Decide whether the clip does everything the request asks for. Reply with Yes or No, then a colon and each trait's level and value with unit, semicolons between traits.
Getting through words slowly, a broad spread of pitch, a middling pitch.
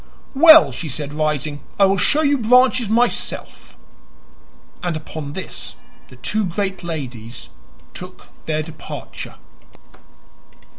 Yes: slow, 110 wpm; wide, 7.0 semitones; medium, 175 Hz